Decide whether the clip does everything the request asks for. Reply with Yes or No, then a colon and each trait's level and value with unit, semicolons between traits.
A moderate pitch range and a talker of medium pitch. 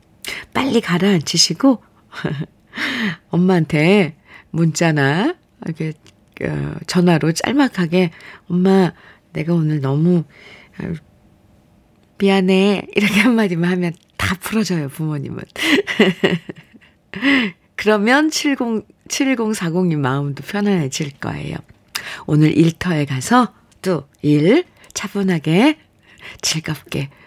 Yes: average, 4.6 semitones; medium, 180 Hz